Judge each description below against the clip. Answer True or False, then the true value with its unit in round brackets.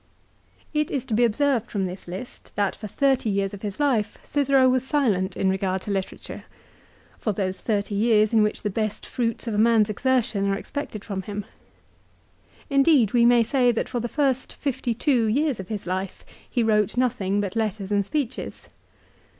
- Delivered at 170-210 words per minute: True (185 wpm)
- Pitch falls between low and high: False (220 Hz)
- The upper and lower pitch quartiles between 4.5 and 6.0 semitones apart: False (4.1 semitones)